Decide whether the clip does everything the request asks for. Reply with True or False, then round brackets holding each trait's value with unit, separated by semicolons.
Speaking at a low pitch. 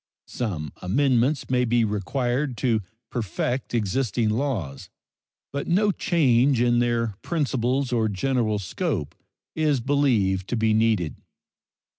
True (120 Hz)